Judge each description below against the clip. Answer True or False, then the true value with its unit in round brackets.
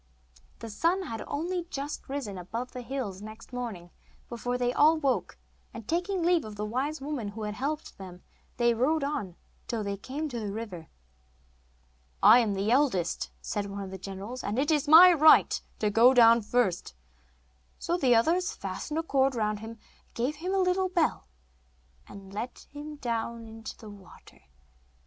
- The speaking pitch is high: True (240 Hz)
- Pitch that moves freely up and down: True (6.0 semitones)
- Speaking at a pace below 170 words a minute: False (175 wpm)